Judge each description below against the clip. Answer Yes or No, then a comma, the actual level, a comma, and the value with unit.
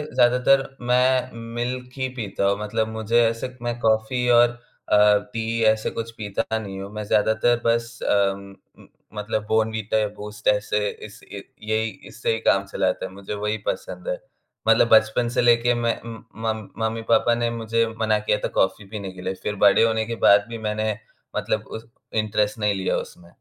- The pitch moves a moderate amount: No, narrow, 2.0 semitones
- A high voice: No, low, 110 Hz